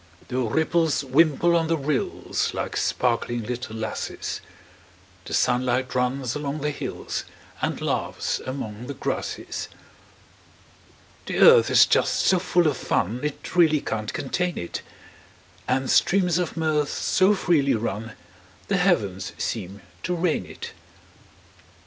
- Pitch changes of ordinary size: No, wide, 5.7 semitones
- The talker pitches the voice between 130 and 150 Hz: Yes, medium, 140 Hz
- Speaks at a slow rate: Yes, slow, 130 wpm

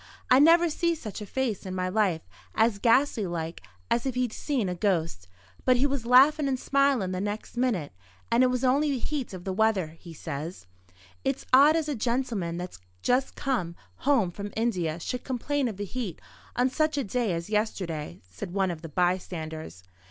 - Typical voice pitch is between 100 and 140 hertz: No, high, 220 Hz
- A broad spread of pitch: Yes, wide, 6.6 semitones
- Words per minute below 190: No, average, 195 wpm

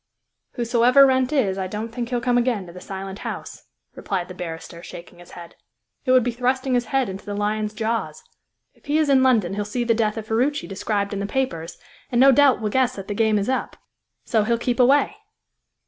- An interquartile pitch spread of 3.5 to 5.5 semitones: Yes, average, 4.2 semitones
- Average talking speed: No, fast, 220 wpm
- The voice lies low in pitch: No, high, 230 Hz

